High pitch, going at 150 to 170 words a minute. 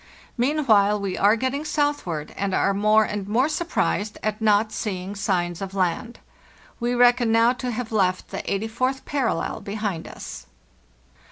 Yes: high, 215 Hz; average, 160 wpm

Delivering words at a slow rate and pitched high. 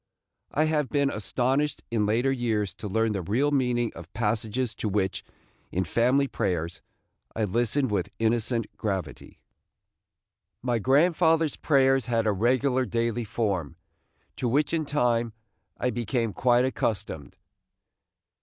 No: slow, 130 wpm; low, 120 Hz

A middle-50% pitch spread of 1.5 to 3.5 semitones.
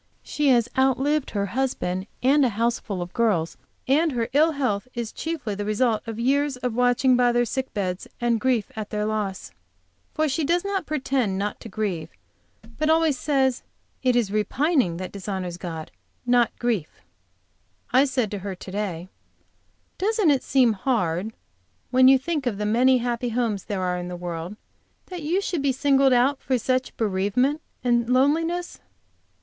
No: average, 4.8 semitones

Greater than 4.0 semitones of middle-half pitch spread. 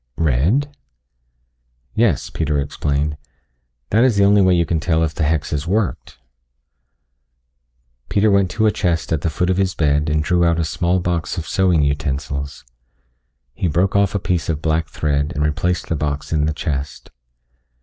No: average, 3.7 semitones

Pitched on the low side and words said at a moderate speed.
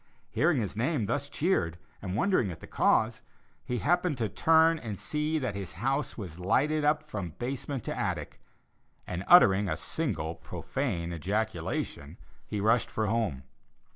Yes: low, 115 Hz; average, 155 wpm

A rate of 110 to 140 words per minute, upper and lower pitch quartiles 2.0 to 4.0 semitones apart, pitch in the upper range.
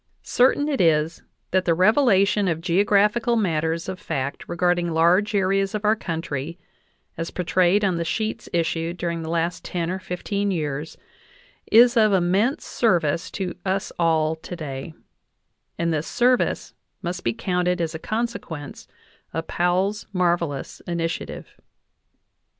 No: slow, 135 wpm; average, 3.4 semitones; medium, 175 Hz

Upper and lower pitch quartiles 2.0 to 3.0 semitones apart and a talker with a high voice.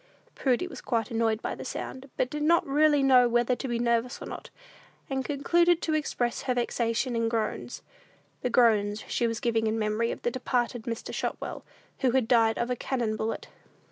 Yes: narrow, 2.6 semitones; high, 240 Hz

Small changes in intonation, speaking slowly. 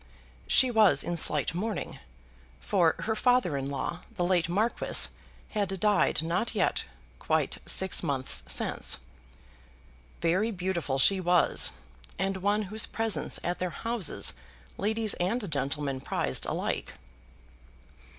No: average, 4.7 semitones; slow, 125 wpm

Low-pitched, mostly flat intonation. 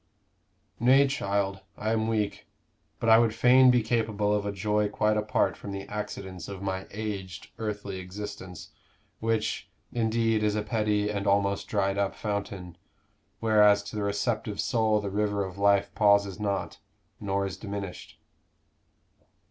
Yes: low, 105 Hz; narrow, 1.6 semitones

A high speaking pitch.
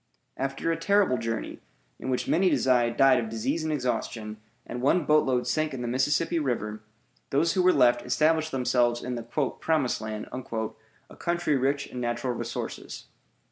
No: low, 130 Hz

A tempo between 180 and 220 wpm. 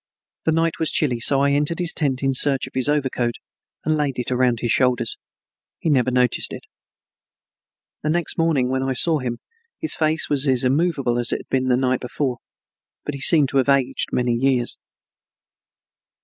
Yes: average, 190 wpm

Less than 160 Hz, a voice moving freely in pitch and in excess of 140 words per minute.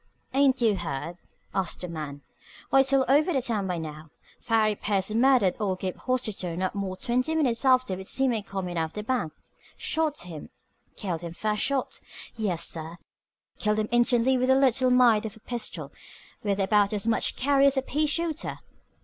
No: high, 215 Hz; wide, 5.7 semitones; average, 185 wpm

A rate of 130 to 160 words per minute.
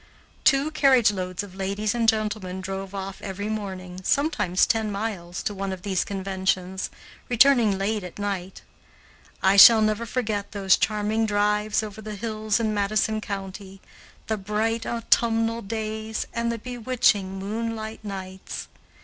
Yes: average, 140 wpm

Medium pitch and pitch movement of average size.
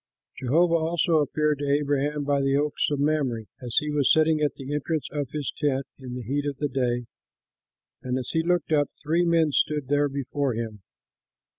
No: medium, 145 Hz; narrow, 2.1 semitones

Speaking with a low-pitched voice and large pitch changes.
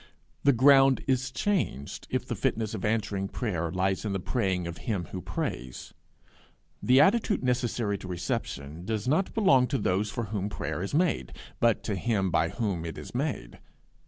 Yes: low, 105 Hz; wide, 5.9 semitones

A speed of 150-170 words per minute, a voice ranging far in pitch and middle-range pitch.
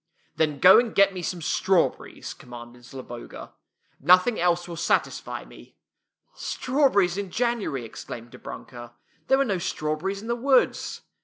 Yes: average, 155 wpm; wide, 7.5 semitones; medium, 180 Hz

